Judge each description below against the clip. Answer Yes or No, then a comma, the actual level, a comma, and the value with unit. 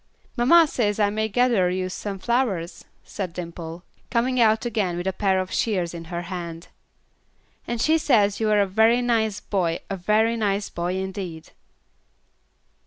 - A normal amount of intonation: Yes, average, 4.0 semitones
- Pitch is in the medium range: No, high, 200 Hz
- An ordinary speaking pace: Yes, average, 165 wpm